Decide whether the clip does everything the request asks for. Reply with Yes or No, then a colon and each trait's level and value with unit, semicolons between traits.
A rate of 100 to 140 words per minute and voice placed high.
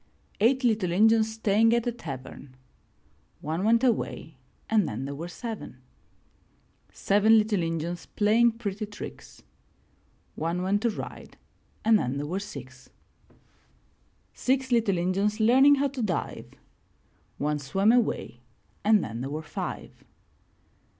Yes: slow, 135 wpm; high, 205 Hz